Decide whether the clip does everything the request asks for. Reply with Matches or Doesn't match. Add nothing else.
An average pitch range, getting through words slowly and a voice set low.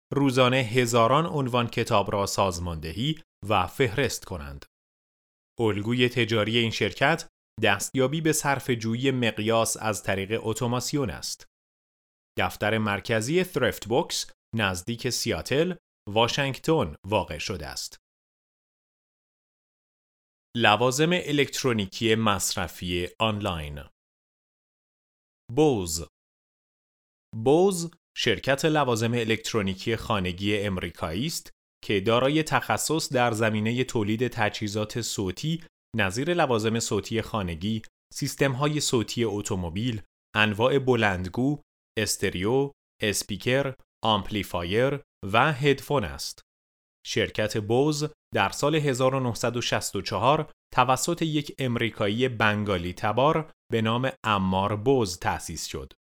Matches